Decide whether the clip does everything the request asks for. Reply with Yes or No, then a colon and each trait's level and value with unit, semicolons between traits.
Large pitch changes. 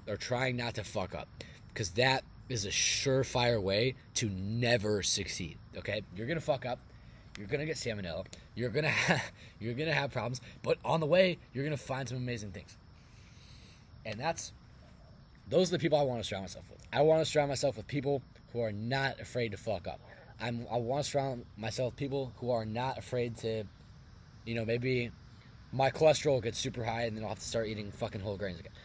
No: average, 3.7 semitones